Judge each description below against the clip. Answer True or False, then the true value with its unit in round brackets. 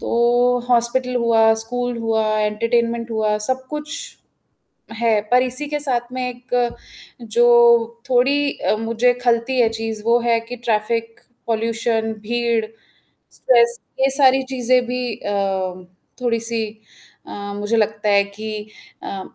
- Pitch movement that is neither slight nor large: False (1.7 semitones)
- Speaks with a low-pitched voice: False (235 Hz)